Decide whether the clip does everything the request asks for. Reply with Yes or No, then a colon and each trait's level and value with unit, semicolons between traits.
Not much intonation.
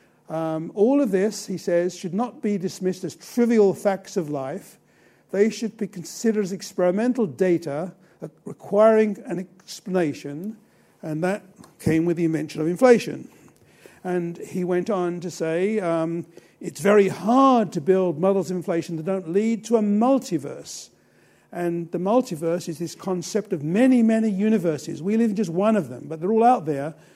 No: average, 4.0 semitones